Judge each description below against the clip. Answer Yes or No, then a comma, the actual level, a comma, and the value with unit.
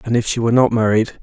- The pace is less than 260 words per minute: No, fast, 295 wpm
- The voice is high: No, low, 115 Hz